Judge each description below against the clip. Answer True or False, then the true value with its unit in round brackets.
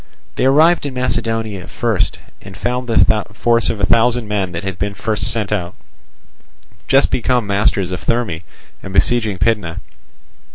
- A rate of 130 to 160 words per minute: True (155 wpm)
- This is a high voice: False (110 Hz)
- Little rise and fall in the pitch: False (3.7 semitones)